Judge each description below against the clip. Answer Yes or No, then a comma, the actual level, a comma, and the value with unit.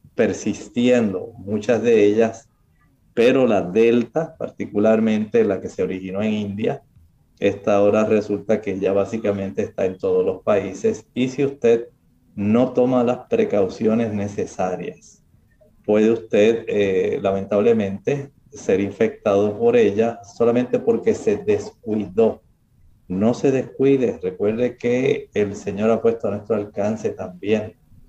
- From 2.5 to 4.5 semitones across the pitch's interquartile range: Yes, average, 3.3 semitones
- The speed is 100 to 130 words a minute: Yes, slow, 125 wpm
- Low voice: Yes, low, 110 Hz